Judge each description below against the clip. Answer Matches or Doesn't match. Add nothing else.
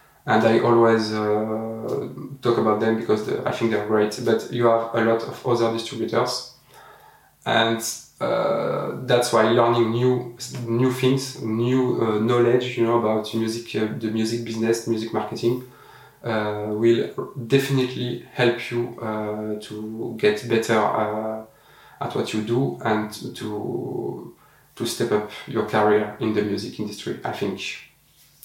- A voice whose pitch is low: Matches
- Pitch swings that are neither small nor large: Doesn't match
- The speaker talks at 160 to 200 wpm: Doesn't match